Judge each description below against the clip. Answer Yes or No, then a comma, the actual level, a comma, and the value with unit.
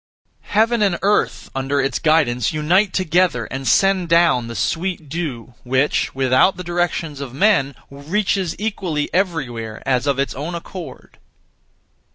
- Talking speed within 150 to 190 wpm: No, average, 140 wpm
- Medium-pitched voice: Yes, medium, 155 Hz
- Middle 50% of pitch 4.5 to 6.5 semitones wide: Yes, wide, 5.5 semitones